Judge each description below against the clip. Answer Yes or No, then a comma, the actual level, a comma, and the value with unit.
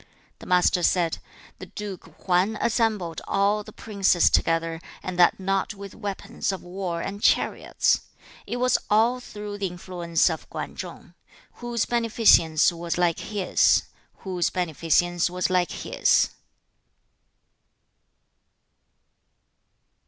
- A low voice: No, medium, 185 Hz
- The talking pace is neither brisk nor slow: No, slow, 115 wpm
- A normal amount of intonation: Yes, average, 3.1 semitones